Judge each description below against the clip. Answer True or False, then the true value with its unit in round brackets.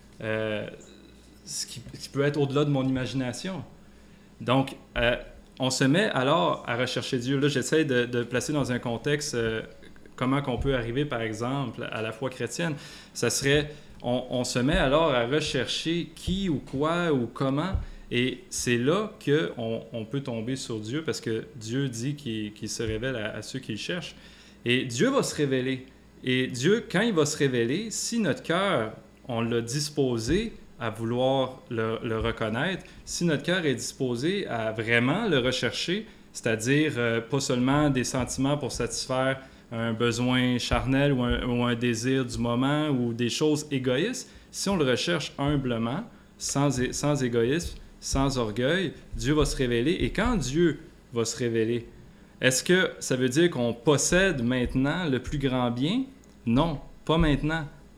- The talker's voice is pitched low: True (130 Hz)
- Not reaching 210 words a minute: True (175 wpm)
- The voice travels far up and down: False (3.9 semitones)